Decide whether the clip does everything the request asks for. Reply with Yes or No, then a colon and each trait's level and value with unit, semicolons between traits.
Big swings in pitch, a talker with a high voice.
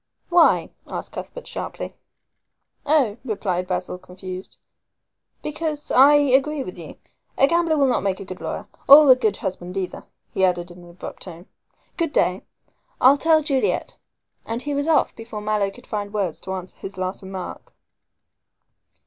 Yes: wide, 7.6 semitones; high, 215 Hz